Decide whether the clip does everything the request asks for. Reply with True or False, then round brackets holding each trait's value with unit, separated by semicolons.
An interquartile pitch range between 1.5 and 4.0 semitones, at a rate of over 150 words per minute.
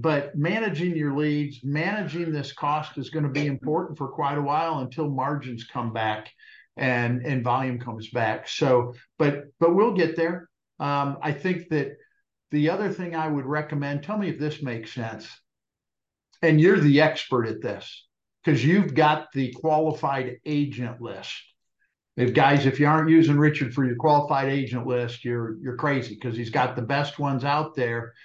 True (3.7 semitones; 175 wpm)